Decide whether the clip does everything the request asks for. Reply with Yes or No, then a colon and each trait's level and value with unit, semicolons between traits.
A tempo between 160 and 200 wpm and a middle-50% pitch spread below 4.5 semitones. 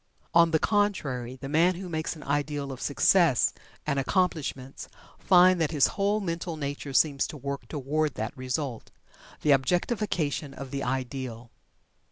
No: average, 150 wpm; average, 4.0 semitones